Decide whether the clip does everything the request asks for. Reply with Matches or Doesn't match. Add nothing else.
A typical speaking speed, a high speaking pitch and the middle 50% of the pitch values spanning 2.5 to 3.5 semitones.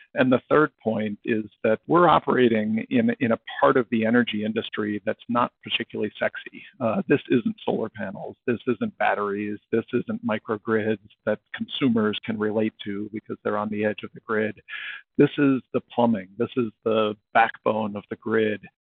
Doesn't match